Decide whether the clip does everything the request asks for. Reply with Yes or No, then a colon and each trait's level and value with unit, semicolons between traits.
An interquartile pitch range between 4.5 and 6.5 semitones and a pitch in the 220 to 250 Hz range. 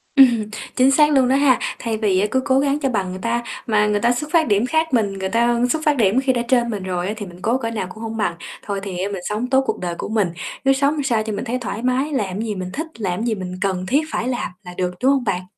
Yes: average, 5.0 semitones; high, 230 Hz